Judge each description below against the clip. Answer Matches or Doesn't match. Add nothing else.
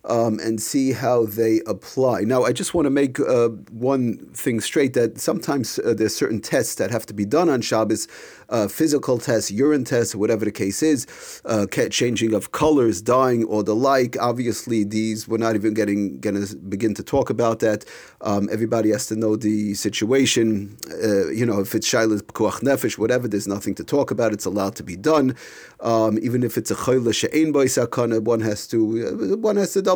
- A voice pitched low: Matches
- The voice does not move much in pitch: Doesn't match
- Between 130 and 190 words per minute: Doesn't match